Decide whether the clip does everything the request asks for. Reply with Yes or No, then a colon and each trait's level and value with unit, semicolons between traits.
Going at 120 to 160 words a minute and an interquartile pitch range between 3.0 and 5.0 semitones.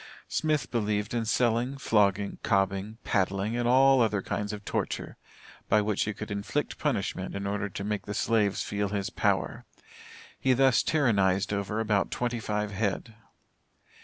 No: average, 155 wpm; narrow, 2.6 semitones